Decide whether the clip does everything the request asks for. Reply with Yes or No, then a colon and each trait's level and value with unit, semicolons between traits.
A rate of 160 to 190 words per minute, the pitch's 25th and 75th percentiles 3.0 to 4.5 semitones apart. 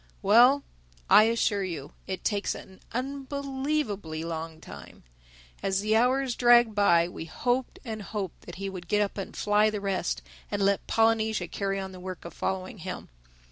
Yes: average, 170 wpm; average, 3.9 semitones